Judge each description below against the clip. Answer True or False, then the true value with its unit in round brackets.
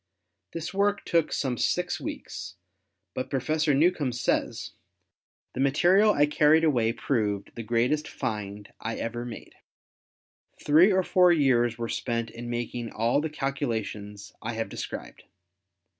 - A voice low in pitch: True (125 Hz)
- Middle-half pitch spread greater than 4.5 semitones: True (5.1 semitones)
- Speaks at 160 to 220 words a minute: False (135 wpm)